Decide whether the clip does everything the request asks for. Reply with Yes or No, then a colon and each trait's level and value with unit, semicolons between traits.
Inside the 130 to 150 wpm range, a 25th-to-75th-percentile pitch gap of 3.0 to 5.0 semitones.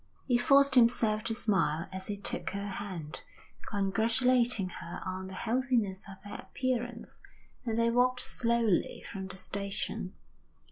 Yes: average, 140 wpm; average, 4.0 semitones